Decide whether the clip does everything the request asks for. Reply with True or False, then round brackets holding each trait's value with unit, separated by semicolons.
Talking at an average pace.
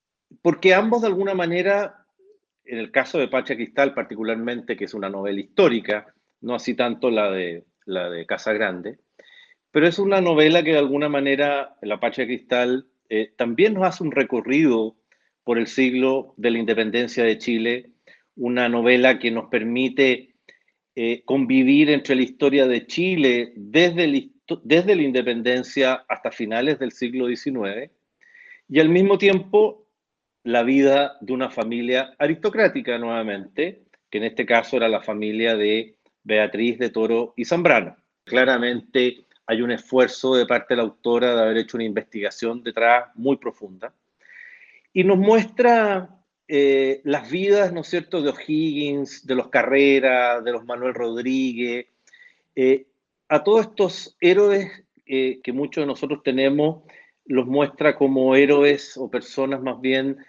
True (150 wpm)